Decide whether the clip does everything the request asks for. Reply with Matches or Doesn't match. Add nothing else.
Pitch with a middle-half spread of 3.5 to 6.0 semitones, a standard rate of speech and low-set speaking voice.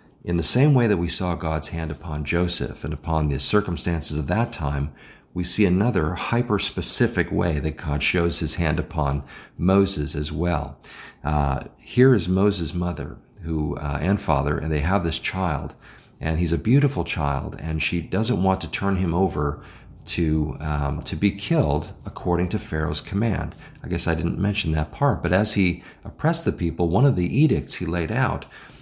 Matches